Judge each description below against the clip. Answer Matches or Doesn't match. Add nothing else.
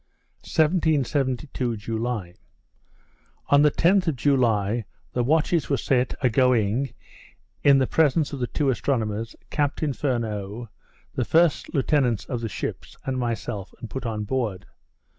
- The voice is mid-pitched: Doesn't match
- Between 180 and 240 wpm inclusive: Doesn't match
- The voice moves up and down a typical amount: Matches